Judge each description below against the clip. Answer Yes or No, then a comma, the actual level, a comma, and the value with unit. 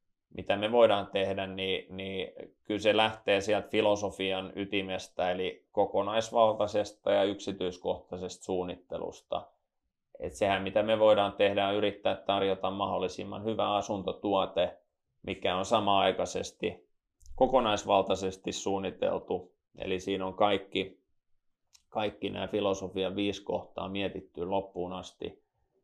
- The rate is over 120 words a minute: No, average, 105 wpm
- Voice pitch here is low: Yes, low, 100 Hz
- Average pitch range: No, narrow, 1.6 semitones